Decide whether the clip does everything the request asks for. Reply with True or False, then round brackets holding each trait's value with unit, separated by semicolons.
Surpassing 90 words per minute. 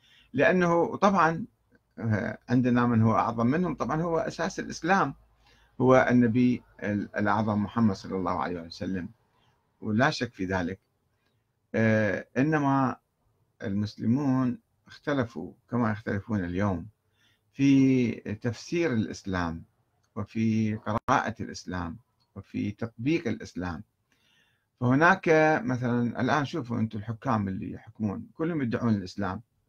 True (100 wpm)